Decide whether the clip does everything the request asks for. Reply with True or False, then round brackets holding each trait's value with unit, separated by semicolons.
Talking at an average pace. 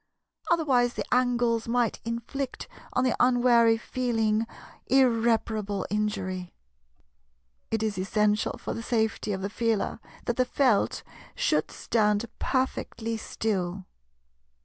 False (110 wpm)